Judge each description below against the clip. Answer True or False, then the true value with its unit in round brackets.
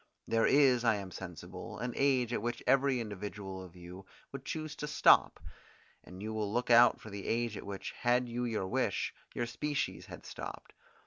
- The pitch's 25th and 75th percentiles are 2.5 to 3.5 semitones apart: False (4.0 semitones)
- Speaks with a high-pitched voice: False (115 Hz)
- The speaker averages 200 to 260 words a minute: False (190 wpm)